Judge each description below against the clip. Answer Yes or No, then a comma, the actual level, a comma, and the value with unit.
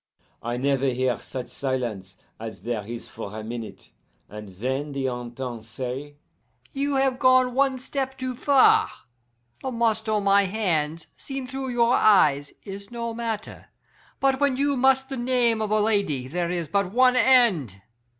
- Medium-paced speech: Yes, average, 160 wpm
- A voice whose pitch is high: Yes, high, 200 Hz